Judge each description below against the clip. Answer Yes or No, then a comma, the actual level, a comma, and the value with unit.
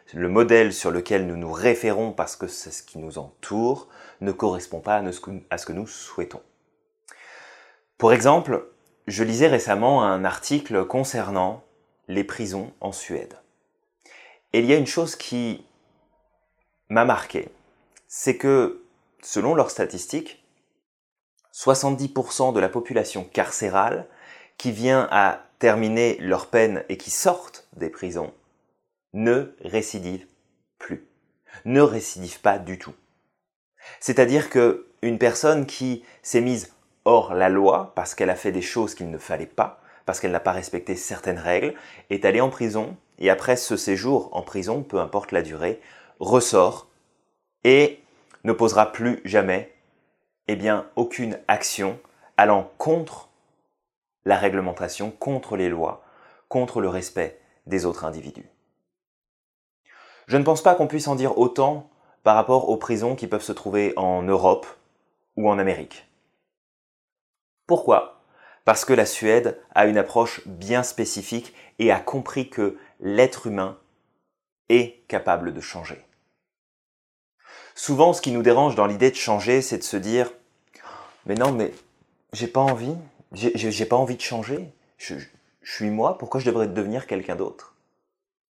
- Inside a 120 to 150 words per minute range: Yes, slow, 145 wpm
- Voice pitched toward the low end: Yes, low, 115 Hz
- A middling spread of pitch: Yes, average, 4.9 semitones